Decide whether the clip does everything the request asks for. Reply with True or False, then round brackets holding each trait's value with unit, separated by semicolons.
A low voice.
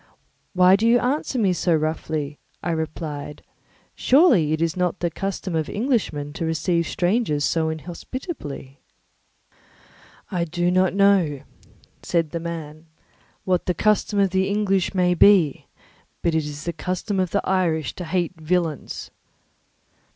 False (175 Hz)